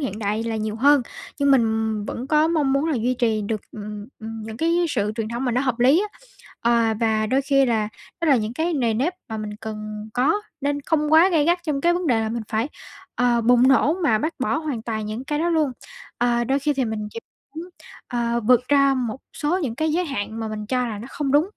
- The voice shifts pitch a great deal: No, average, 4.8 semitones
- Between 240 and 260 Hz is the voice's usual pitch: Yes, high, 245 Hz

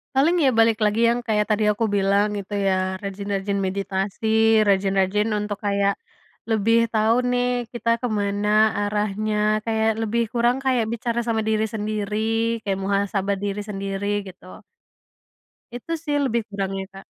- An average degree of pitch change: No, narrow, 2.3 semitones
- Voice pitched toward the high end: Yes, high, 210 Hz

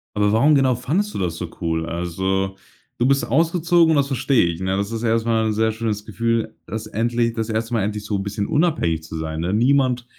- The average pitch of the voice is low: Yes, low, 110 Hz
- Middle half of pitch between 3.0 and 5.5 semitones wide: Yes, average, 4.6 semitones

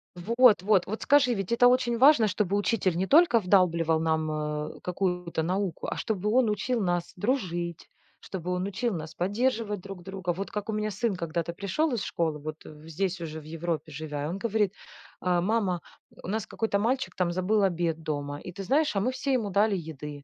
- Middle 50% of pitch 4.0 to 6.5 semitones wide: Yes, average, 4.6 semitones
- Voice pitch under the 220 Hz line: Yes, high, 190 Hz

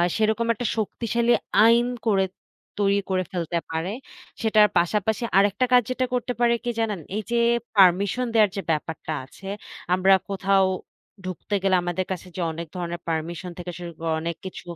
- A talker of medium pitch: No, high, 195 Hz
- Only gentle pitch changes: No, average, 3.8 semitones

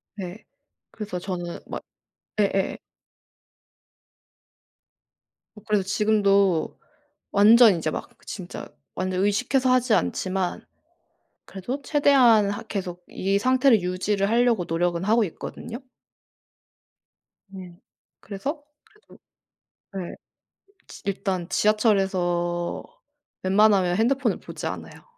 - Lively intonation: No, average, 3.4 semitones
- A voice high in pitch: Yes, high, 200 Hz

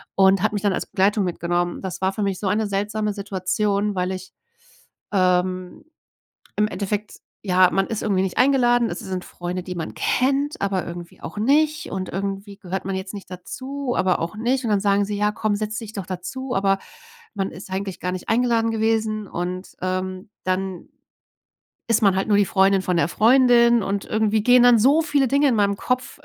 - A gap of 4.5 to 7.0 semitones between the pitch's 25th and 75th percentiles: No, average, 3.2 semitones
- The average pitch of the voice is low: No, high, 200 Hz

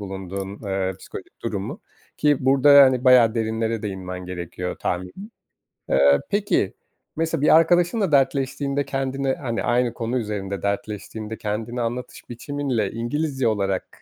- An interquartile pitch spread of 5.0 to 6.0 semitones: Yes, wide, 5.6 semitones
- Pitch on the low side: Yes, low, 115 Hz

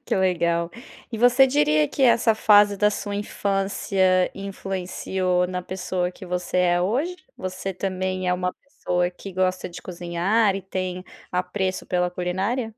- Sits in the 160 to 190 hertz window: Yes, medium, 185 Hz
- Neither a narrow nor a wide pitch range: No, narrow, 2.0 semitones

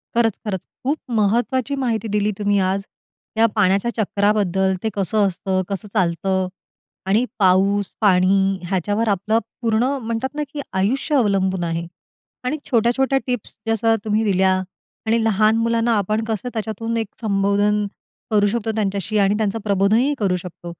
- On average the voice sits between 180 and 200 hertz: No, high, 210 Hz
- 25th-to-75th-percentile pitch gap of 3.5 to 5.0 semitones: No, average, 2.7 semitones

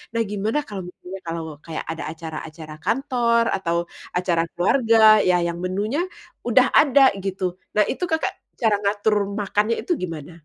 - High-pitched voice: Yes, high, 195 Hz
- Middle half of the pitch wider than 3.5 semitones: Yes, average, 5.1 semitones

